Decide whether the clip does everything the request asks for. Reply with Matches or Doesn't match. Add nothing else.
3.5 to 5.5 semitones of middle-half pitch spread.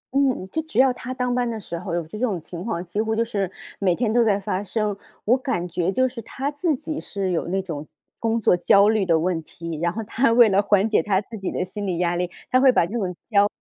Matches